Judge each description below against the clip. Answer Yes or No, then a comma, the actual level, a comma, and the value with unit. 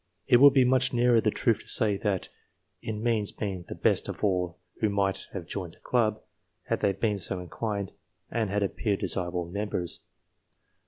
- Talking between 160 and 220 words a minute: Yes, average, 180 wpm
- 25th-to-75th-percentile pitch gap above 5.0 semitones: No, average, 3.2 semitones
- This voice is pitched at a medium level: No, low, 105 Hz